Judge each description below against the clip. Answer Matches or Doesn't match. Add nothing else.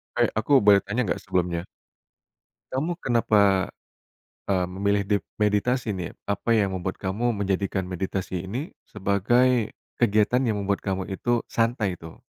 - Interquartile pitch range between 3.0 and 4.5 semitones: Matches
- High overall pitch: Doesn't match